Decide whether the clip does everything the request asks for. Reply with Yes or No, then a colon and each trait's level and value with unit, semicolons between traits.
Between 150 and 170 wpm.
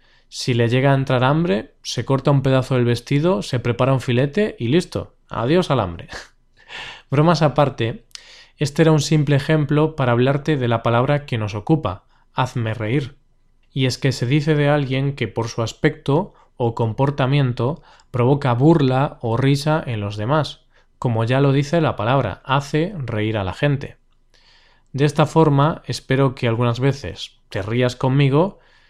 Yes: average, 165 wpm